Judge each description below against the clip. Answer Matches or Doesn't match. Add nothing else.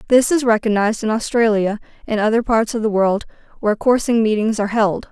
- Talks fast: Doesn't match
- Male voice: Doesn't match